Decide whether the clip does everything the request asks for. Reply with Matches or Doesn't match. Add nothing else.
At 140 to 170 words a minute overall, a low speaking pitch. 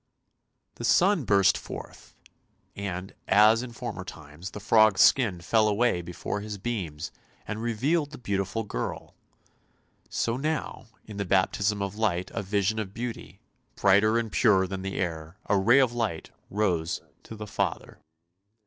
Matches